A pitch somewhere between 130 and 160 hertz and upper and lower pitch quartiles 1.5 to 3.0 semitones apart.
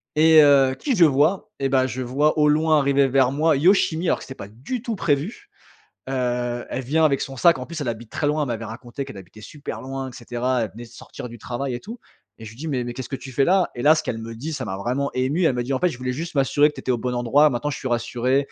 No: low, 135 Hz; average, 3.9 semitones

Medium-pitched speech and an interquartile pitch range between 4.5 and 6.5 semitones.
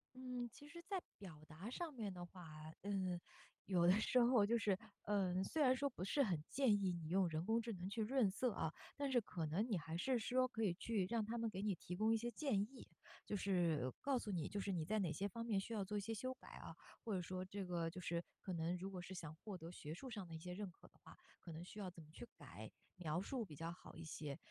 No: high, 195 Hz; average, 4.8 semitones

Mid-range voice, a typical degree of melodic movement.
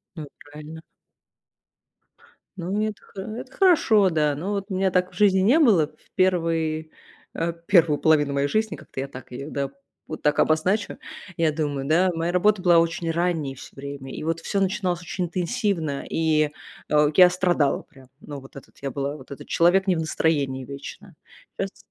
Yes: medium, 165 Hz; average, 4.2 semitones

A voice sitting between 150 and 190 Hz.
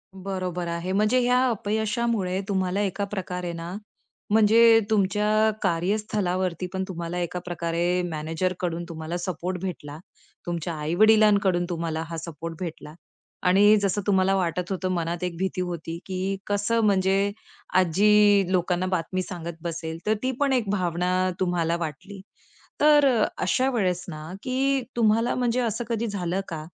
Yes: medium, 185 Hz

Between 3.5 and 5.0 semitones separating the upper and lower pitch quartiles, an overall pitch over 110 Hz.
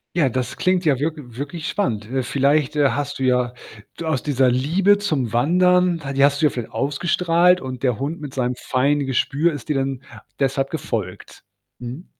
Yes: average, 4.0 semitones; medium, 140 Hz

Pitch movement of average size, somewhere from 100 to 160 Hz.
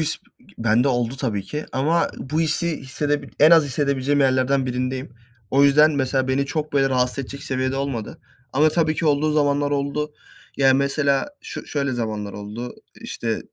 No: narrow, 2.2 semitones; medium, 140 Hz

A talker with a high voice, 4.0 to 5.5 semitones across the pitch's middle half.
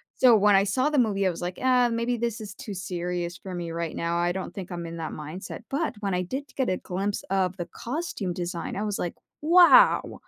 Yes: high, 195 Hz; average, 4.9 semitones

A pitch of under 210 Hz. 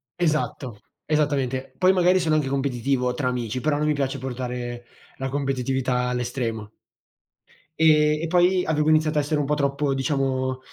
Yes: low, 135 Hz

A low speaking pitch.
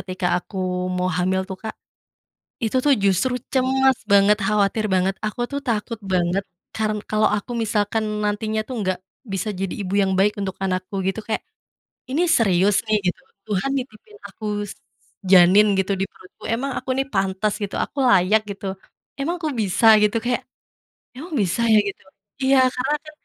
No: high, 210 Hz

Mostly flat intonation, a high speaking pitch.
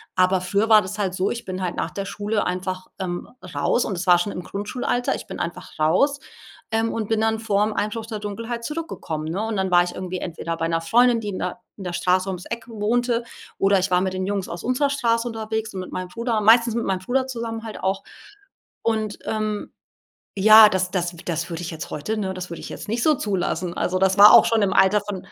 No: average, 3.5 semitones; high, 205 Hz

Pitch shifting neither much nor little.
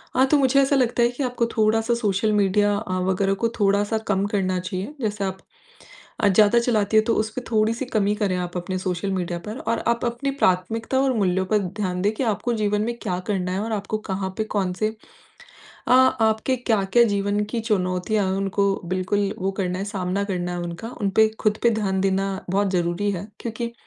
Yes: average, 3.0 semitones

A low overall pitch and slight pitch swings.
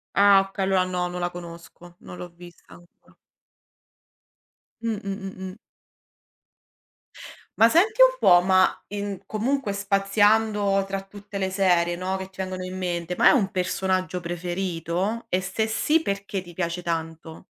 No: high, 190 Hz; narrow, 2.3 semitones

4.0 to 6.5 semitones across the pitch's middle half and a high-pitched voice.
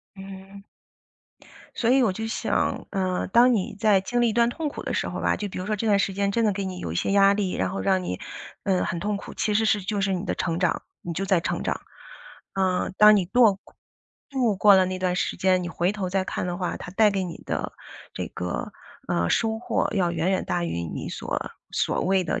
No: narrow, 2.4 semitones; high, 195 Hz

